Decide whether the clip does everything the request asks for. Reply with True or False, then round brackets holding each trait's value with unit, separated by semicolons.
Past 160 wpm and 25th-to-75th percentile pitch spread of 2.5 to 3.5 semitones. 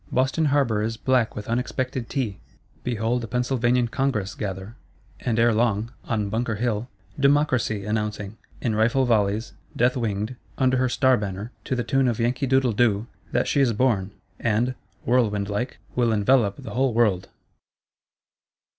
False (155 wpm; 3.2 semitones)